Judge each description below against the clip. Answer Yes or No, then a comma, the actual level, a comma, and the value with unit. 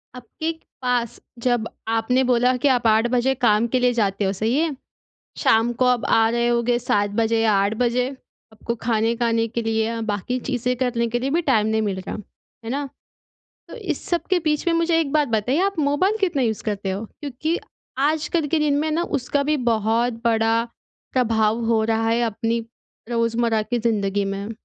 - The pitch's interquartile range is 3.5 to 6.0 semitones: No, average, 2.8 semitones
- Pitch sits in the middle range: No, high, 235 Hz